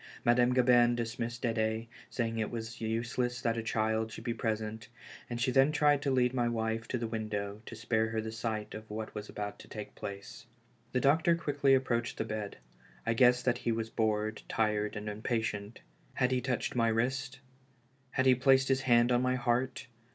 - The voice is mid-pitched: No, low, 115 Hz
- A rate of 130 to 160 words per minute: No, average, 195 wpm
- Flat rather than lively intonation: Yes, narrow, 2.3 semitones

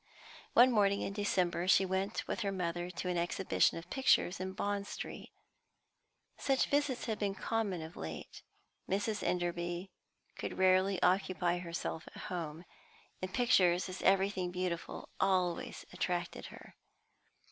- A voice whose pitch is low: No, medium, 185 Hz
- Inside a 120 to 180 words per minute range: Yes, slow, 135 wpm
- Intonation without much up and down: Yes, narrow, 2.1 semitones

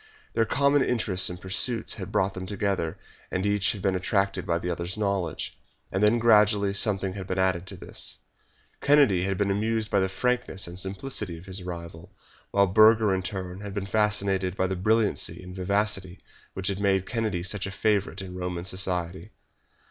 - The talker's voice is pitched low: Yes, very low, 95 Hz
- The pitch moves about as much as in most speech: No, narrow, 2.3 semitones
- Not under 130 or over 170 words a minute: No, average, 185 wpm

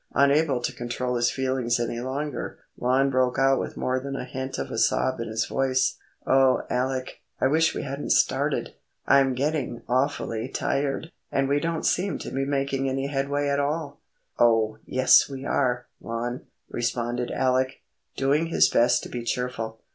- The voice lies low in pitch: Yes, low, 130 Hz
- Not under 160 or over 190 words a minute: Yes, average, 170 wpm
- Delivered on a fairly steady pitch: Yes, narrow, 2.1 semitones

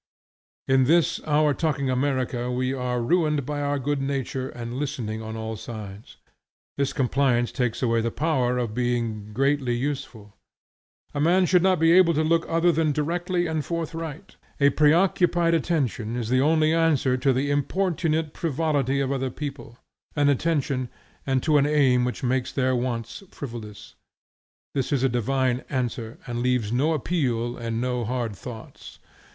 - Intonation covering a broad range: No, average, 3.9 semitones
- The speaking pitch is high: No, low, 135 Hz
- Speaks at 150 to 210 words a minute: Yes, average, 160 wpm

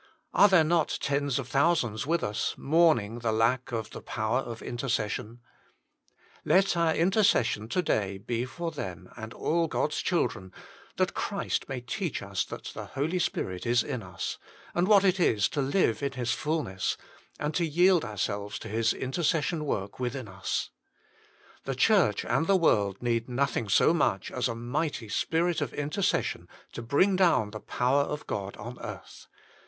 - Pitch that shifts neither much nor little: No, wide, 6.8 semitones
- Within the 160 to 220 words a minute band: Yes, average, 170 wpm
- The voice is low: Yes, low, 130 Hz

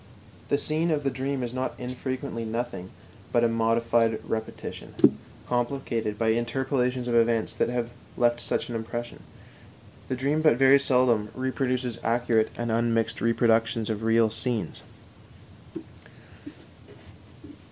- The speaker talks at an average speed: No, slow, 125 wpm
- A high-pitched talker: No, low, 120 Hz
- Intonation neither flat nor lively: No, narrow, 2.1 semitones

